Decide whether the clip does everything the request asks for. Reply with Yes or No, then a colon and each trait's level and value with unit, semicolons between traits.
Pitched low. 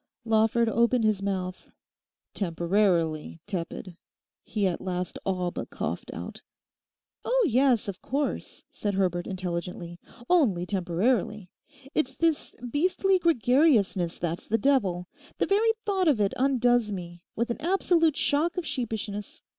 No: high, 215 Hz